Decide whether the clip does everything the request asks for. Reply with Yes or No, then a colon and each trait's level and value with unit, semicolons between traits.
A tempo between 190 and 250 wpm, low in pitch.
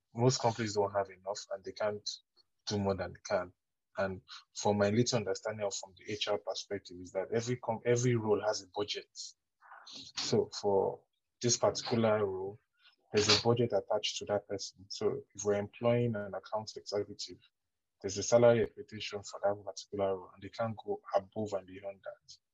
No: average, 180 wpm; low, 105 Hz